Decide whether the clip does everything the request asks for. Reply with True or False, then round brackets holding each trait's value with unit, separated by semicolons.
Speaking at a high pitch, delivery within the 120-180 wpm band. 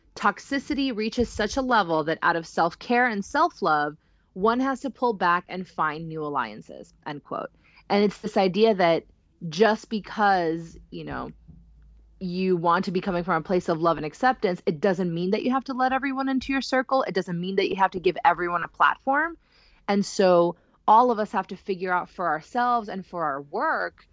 False (195 Hz; 200 wpm)